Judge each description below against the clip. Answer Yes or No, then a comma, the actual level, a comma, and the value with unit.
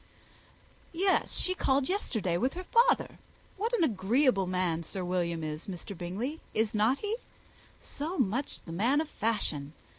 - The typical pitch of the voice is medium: No, high, 225 Hz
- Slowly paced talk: No, average, 150 wpm